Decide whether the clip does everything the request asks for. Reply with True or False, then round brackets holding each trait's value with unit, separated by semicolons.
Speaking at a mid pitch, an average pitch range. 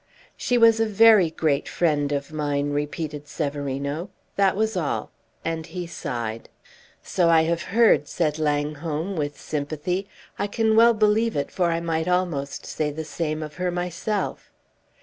True (160 Hz; 4.3 semitones)